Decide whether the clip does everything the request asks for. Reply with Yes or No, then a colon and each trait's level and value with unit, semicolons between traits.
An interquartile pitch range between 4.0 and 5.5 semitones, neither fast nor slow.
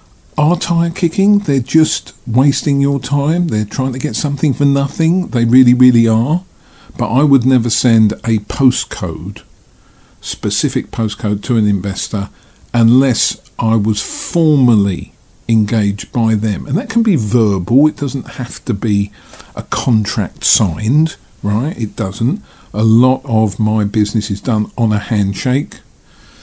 Yes: average, 4.7 semitones; average, 145 wpm